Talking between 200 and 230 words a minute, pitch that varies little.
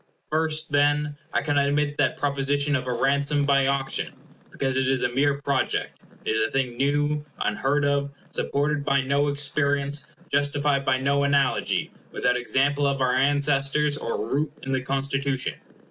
No: average, 165 wpm; narrow, 1.1 semitones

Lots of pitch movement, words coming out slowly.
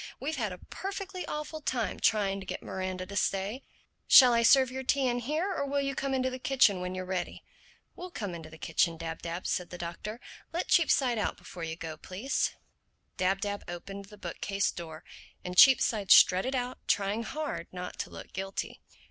No: wide, 6.4 semitones; average, 195 wpm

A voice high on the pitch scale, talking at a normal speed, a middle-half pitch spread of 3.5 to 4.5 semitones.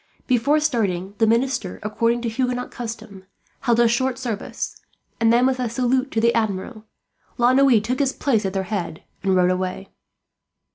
Yes: high, 230 Hz; average, 175 wpm; average, 3.9 semitones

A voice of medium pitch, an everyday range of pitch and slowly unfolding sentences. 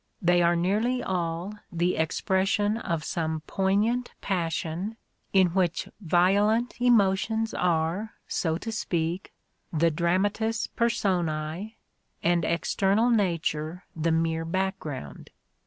Yes: medium, 180 Hz; average, 3.9 semitones; slow, 105 wpm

